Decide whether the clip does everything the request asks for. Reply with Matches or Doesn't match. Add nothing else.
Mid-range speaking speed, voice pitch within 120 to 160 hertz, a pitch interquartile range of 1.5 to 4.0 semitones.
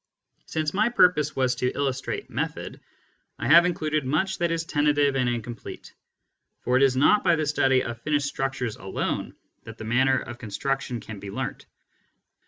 Matches